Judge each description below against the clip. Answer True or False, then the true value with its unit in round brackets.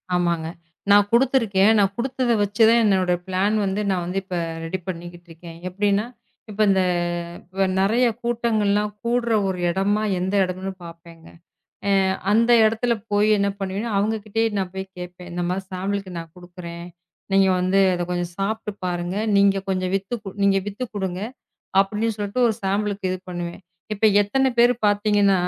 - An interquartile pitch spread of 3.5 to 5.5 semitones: False (2.7 semitones)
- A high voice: True (195 Hz)